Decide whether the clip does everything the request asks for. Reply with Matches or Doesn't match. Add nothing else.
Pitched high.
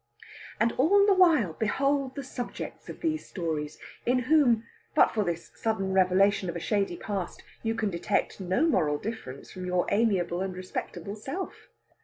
Matches